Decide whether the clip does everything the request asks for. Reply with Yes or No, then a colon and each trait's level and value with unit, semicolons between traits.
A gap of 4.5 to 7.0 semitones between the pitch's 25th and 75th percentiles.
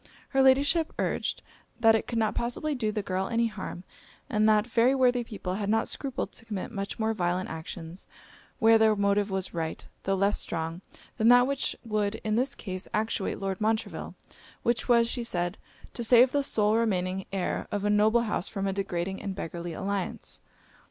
No: average, 3.4 semitones